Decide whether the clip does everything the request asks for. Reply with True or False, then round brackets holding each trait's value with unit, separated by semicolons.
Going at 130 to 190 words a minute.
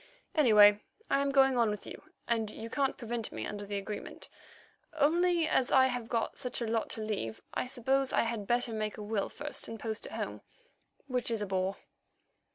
False (200 wpm)